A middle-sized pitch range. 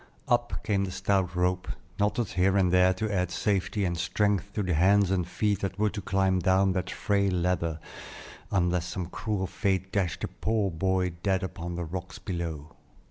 No: narrow, 1.8 semitones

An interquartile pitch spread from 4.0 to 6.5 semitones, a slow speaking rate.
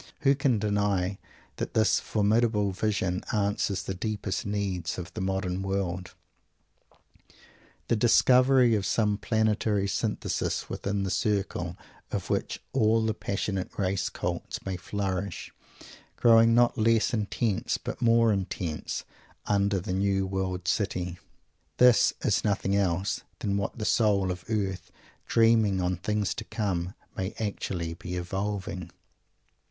No: narrow, 2.6 semitones; slow, 130 wpm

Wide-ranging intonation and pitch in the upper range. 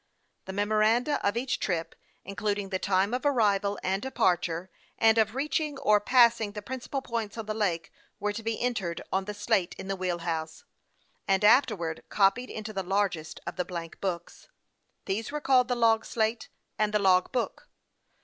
No: average, 3.5 semitones; high, 210 Hz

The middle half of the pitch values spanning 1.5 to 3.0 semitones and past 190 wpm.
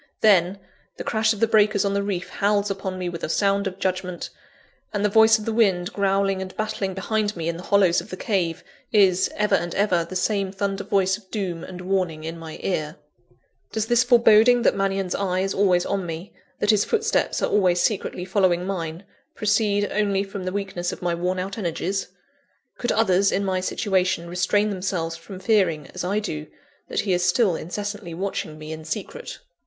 Yes: narrow, 2.4 semitones; average, 200 wpm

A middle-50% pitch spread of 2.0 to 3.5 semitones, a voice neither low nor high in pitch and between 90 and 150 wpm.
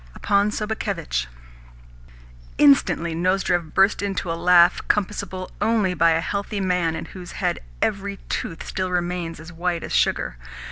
Yes: average, 3.0 semitones; medium, 180 Hz; average, 140 wpm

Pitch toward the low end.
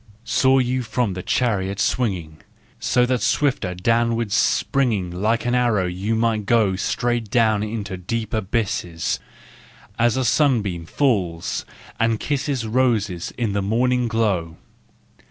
Yes: low, 110 Hz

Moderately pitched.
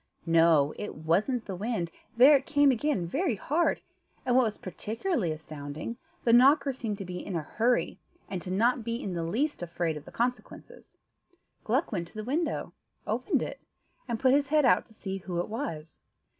No: high, 220 Hz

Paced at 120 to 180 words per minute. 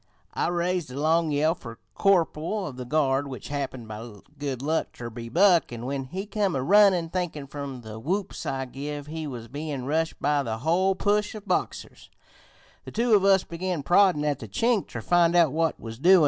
No: fast, 205 wpm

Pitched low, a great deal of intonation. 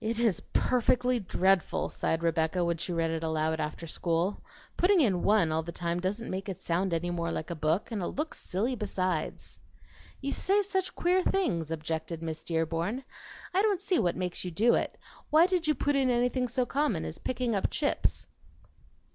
No: high, 190 Hz; wide, 7.3 semitones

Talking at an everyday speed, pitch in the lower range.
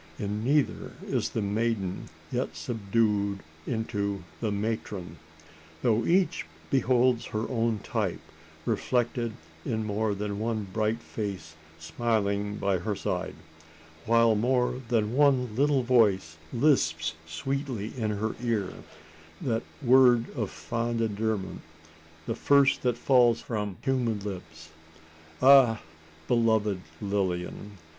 No: slow, 115 wpm; low, 110 Hz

